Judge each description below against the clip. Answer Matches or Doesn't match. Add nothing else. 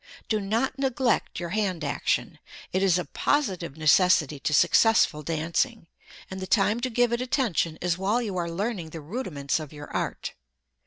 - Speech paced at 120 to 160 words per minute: Doesn't match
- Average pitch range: Doesn't match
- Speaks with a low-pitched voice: Doesn't match